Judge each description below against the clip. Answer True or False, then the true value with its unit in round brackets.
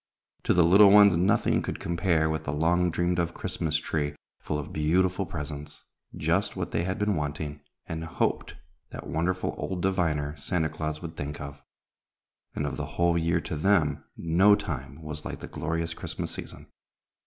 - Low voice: True (80 Hz)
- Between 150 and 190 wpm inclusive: True (175 wpm)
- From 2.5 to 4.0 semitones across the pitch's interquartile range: True (2.8 semitones)